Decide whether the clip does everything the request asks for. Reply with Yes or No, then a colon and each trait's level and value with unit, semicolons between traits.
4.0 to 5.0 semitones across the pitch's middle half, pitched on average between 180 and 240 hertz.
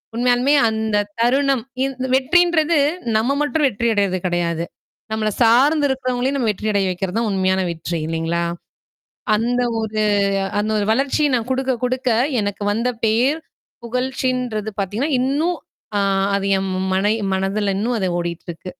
Yes: average, 4.7 semitones; high, 225 Hz